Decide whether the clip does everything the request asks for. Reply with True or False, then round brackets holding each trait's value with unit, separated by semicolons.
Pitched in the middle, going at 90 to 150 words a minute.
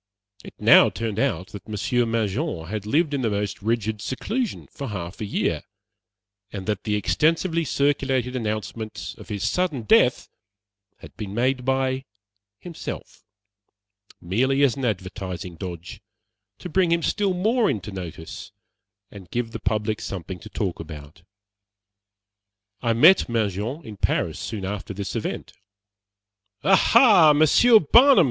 False (115 Hz; 140 wpm)